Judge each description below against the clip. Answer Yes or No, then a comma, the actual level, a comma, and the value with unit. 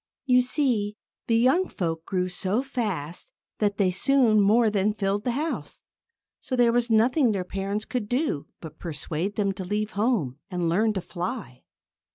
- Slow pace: No, average, 170 wpm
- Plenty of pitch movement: No, average, 4.8 semitones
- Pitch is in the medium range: No, high, 210 Hz